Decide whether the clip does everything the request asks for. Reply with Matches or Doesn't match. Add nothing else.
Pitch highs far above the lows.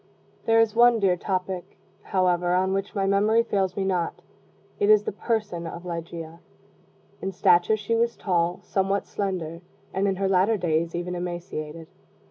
Doesn't match